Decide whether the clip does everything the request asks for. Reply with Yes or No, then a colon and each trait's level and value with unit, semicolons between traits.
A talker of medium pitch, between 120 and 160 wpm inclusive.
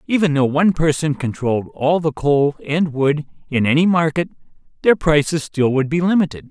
No: medium, 150 Hz; average, 175 wpm